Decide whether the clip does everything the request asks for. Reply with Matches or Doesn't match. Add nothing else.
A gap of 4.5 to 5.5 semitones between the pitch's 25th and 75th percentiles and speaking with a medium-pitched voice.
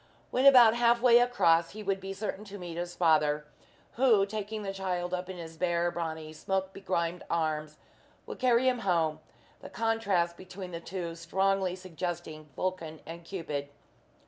Doesn't match